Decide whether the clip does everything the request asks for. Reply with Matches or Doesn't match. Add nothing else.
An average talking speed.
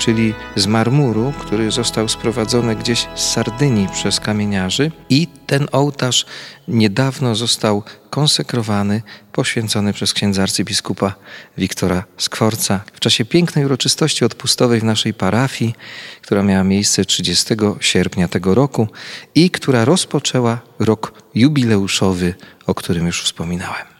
Matches